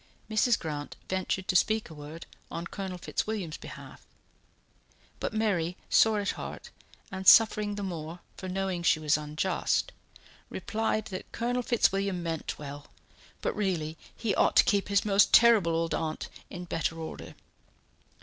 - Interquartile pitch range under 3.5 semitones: No, average, 4.2 semitones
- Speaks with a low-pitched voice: No, medium, 185 Hz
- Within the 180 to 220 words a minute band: No, average, 150 wpm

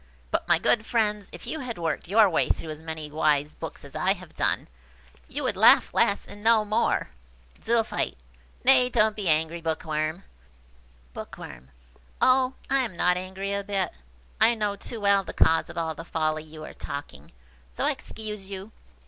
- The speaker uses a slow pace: No, average, 180 wpm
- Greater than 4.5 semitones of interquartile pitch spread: Yes, average, 5.2 semitones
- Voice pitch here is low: No, high, 190 Hz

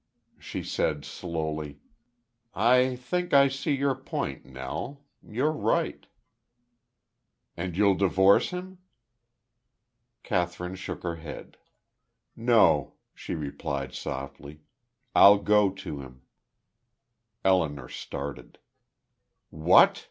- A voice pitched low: Yes, very low, 95 Hz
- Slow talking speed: Yes, slow, 95 wpm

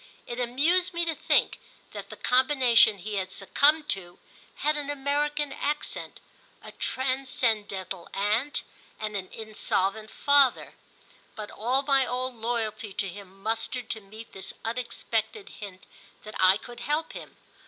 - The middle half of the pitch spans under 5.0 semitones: No, average, 5.3 semitones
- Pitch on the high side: Yes, high, 235 Hz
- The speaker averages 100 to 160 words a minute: Yes, average, 140 wpm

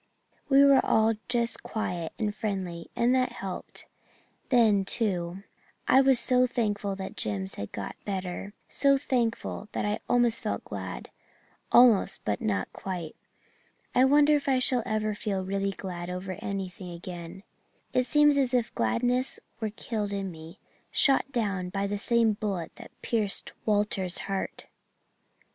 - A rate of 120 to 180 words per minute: Yes, average, 150 wpm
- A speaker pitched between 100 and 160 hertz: No, high, 205 Hz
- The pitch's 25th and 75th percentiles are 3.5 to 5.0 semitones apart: Yes, average, 4.7 semitones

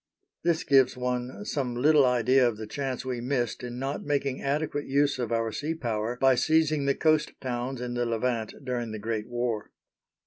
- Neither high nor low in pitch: No, low, 125 Hz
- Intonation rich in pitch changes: No, average, 2.7 semitones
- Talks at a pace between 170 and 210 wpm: Yes, average, 185 wpm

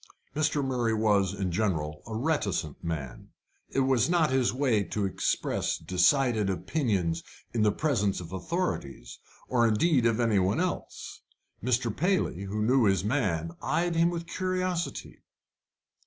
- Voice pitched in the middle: No, low, 110 Hz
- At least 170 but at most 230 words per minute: No, average, 140 wpm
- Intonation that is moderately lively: No, wide, 7.1 semitones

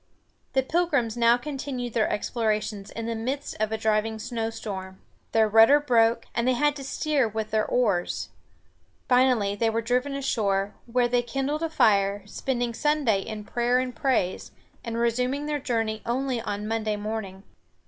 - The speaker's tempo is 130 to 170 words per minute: Yes, average, 160 wpm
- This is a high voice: Yes, high, 230 Hz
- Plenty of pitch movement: No, average, 3.0 semitones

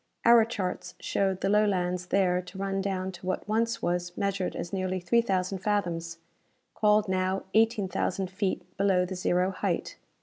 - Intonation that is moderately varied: No, narrow, 1.9 semitones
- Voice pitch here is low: No, high, 190 Hz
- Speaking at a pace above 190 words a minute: No, average, 165 wpm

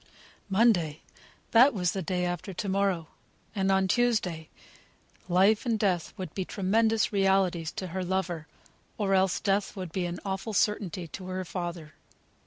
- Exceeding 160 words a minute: No, average, 155 wpm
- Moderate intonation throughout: No, narrow, 2.2 semitones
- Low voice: No, high, 190 Hz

